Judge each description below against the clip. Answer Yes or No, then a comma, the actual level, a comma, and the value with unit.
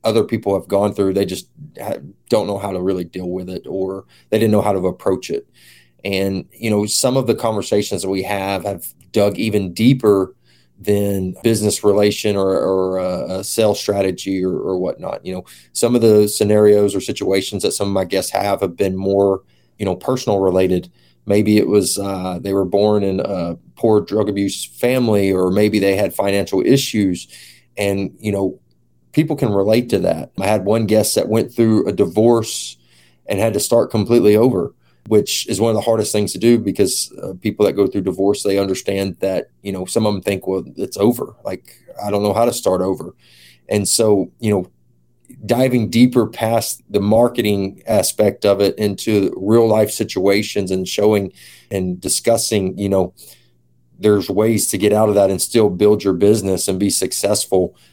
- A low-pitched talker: Yes, low, 100 Hz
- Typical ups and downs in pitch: No, narrow, 2.1 semitones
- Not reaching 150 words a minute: No, average, 190 wpm